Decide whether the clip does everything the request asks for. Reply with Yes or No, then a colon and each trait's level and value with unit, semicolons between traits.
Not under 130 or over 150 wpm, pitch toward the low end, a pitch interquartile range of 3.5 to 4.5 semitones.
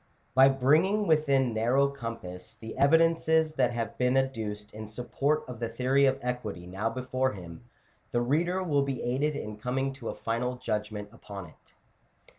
No: average, 165 wpm; low, 125 Hz; average, 3.9 semitones